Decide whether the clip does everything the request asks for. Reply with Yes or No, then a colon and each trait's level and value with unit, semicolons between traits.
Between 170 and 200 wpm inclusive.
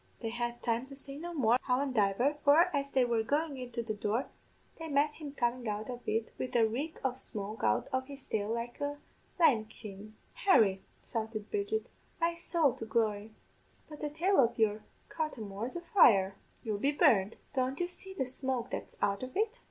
Yes: average, 190 wpm